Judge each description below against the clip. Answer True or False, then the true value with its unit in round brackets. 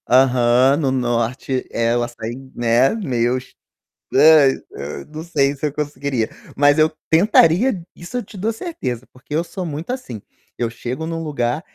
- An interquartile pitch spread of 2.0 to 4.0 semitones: False (4.9 semitones)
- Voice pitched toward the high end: False (135 Hz)